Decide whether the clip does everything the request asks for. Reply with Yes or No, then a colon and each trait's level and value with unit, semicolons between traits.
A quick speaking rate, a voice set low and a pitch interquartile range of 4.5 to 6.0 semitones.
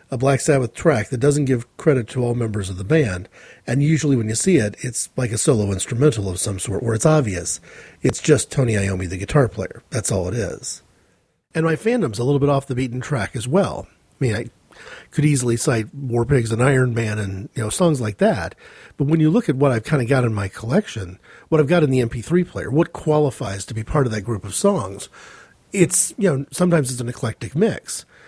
Yes: fast, 230 wpm; low, 130 Hz; wide, 5.4 semitones